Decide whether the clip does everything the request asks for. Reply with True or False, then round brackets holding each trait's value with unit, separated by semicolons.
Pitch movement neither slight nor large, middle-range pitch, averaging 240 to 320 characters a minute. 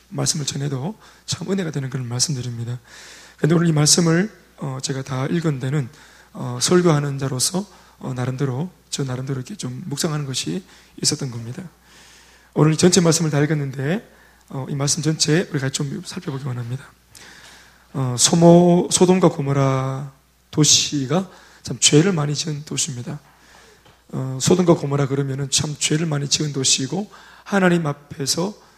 True (4.0 semitones; 145 Hz; 315 characters per minute)